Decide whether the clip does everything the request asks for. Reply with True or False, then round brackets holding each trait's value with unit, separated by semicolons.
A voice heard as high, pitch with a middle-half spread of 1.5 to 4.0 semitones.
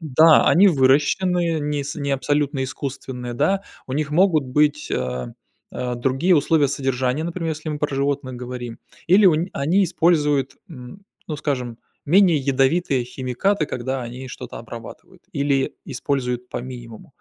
False (140 Hz; 3.7 semitones)